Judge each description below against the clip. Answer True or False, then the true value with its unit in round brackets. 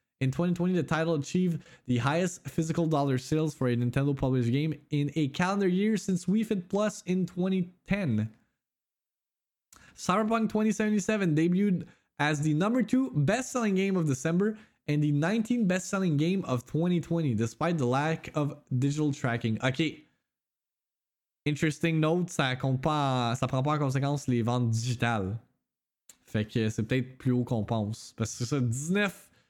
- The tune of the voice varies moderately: False (5.9 semitones)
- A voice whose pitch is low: False (155 Hz)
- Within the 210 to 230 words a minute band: False (150 wpm)